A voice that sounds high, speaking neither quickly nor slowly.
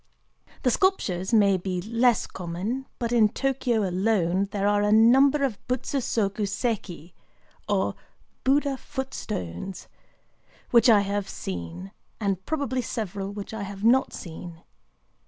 No: high, 210 Hz; slow, 130 wpm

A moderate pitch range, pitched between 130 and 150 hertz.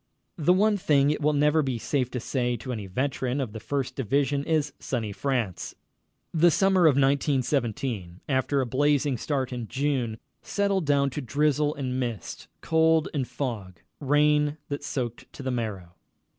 Yes: average, 3.3 semitones; medium, 140 Hz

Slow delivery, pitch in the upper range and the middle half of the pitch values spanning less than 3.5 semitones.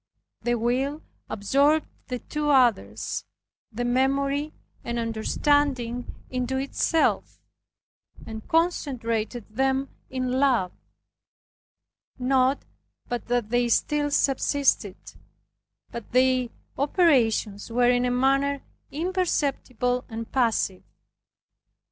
Yes: slow, 90 wpm; very high, 255 Hz; average, 2.9 semitones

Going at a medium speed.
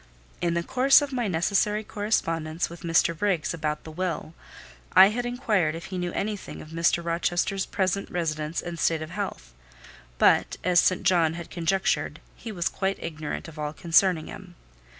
Yes: average, 170 wpm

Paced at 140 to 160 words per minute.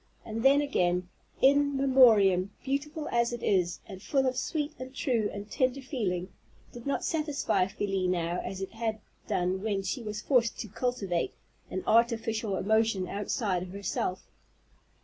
Yes: average, 155 wpm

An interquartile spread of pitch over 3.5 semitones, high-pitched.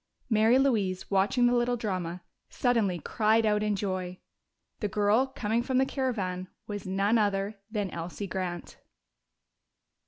Yes: average, 3.9 semitones; high, 210 Hz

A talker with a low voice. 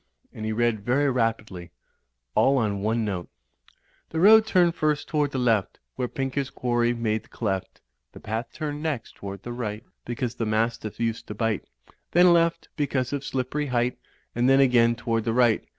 Yes: low, 120 Hz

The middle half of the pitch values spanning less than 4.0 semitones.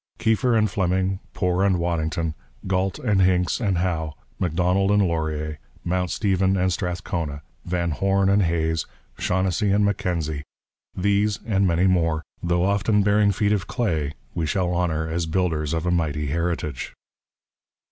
Yes: average, 3.0 semitones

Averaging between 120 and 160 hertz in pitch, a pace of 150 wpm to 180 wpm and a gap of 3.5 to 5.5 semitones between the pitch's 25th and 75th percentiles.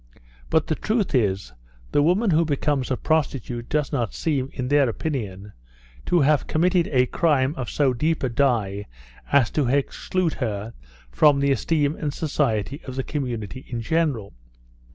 Yes: medium, 140 Hz; average, 160 wpm; average, 4.4 semitones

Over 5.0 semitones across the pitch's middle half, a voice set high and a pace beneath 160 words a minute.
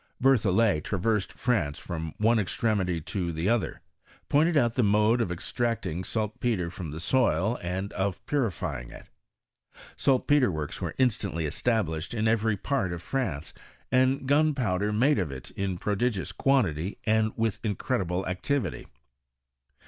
No: wide, 5.4 semitones; low, 105 Hz; average, 145 wpm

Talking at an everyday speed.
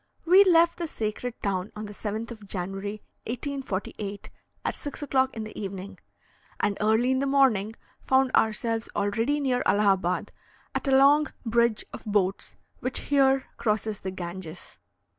Yes: average, 150 wpm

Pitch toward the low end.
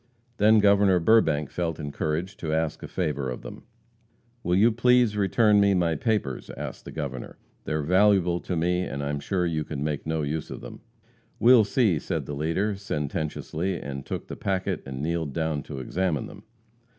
Yes: very low, 85 Hz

